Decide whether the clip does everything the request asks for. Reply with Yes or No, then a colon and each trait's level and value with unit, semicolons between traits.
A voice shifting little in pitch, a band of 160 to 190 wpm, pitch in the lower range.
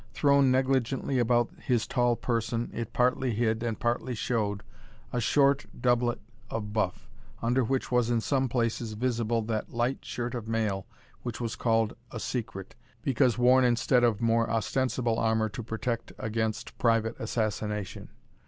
No: narrow, 1.8 semitones; average, 150 wpm; low, 120 Hz